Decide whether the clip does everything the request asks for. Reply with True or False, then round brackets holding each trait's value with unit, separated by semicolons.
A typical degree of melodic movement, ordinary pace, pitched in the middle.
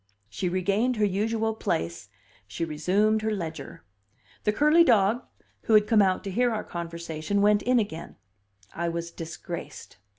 False (4.6 semitones; 155 wpm; 200 Hz)